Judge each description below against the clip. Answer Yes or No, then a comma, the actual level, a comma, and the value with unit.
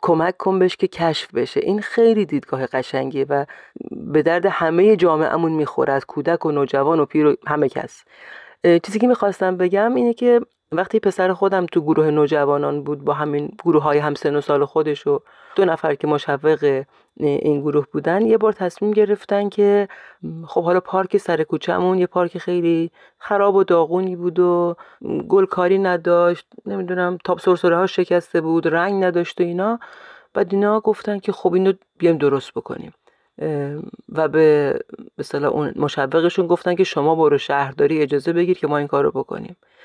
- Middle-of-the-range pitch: Yes, medium, 175 Hz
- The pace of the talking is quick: Yes, fast, 165 wpm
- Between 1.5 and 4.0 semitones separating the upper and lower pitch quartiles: No, average, 4.5 semitones